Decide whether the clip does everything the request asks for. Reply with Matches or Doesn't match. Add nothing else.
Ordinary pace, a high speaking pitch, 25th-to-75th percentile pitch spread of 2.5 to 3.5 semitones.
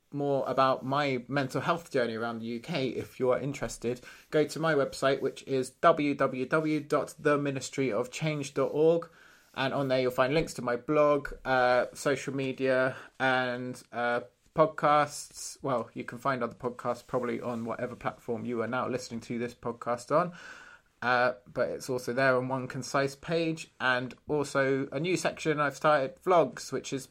Doesn't match